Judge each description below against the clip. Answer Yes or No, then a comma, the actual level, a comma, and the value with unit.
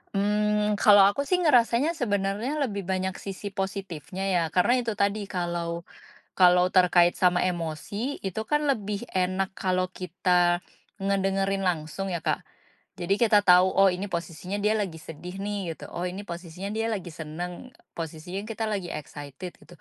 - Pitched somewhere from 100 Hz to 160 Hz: No, high, 190 Hz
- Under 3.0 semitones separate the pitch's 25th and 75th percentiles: Yes, narrow, 2.6 semitones